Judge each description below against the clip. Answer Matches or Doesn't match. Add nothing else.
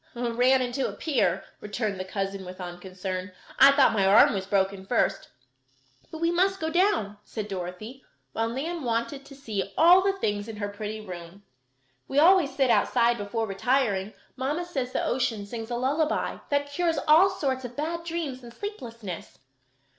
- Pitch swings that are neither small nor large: Doesn't match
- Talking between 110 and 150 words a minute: Doesn't match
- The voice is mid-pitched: Doesn't match